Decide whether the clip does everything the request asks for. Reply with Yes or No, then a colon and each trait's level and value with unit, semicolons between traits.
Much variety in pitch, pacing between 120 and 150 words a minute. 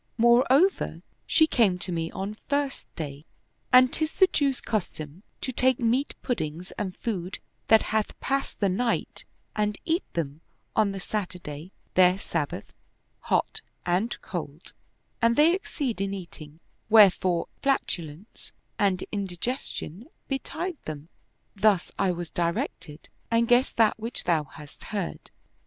Yes: wide, 6.0 semitones; average, 140 wpm